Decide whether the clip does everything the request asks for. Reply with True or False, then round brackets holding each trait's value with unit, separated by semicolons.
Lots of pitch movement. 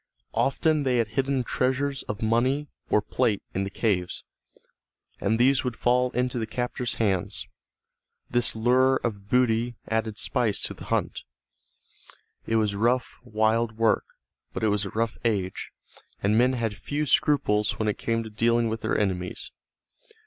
False (2.9 semitones)